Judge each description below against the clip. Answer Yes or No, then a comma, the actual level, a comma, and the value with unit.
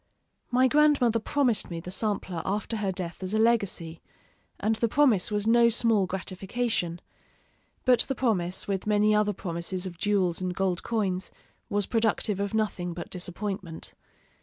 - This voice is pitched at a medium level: No, high, 205 Hz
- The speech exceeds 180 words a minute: No, average, 155 wpm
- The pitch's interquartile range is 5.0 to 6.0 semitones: No, average, 3.7 semitones